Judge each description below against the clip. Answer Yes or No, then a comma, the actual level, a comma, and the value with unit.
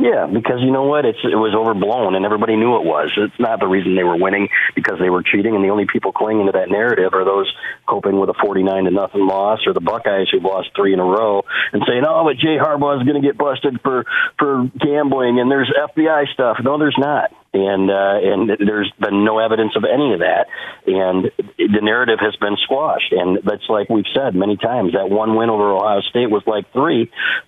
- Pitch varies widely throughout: No, average, 4.6 semitones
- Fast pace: Yes, fast, 225 wpm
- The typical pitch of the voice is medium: No, low, 105 Hz